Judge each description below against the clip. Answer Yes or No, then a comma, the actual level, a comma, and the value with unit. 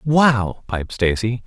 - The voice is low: Yes, low, 115 Hz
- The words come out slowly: Yes, slow, 125 wpm